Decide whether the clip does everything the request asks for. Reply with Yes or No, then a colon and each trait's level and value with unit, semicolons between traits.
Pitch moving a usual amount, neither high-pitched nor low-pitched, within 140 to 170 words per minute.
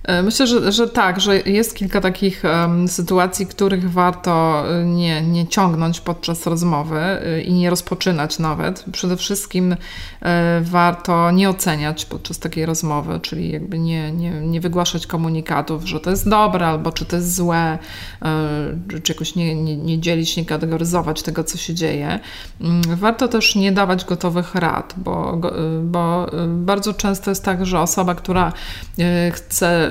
No: narrow, 2.2 semitones; medium, 175 Hz; average, 145 wpm